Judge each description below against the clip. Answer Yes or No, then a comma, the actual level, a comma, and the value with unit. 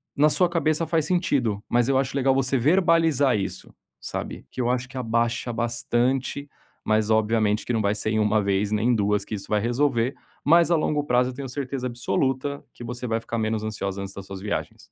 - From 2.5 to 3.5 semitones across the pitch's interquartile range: No, average, 4.2 semitones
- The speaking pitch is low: Yes, low, 120 Hz